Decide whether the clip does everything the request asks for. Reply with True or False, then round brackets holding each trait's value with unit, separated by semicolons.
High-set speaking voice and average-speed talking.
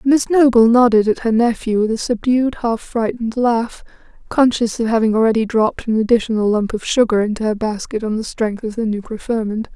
True (225 Hz; 195 wpm)